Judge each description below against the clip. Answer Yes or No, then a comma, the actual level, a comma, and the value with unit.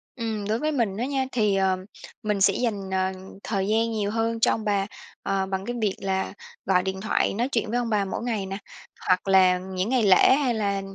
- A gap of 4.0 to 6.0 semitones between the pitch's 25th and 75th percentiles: No, average, 3.0 semitones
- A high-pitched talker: Yes, high, 205 Hz